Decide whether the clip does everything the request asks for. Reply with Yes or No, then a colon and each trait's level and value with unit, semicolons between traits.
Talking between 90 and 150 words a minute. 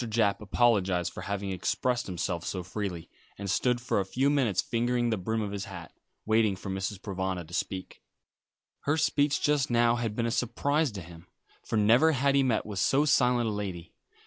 No: average, 195 wpm